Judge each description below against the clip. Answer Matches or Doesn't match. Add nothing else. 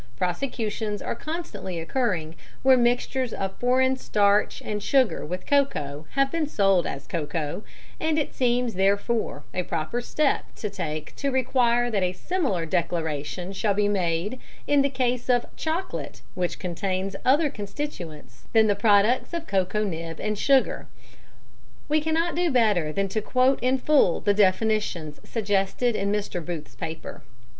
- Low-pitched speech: Doesn't match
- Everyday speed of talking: Matches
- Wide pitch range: Matches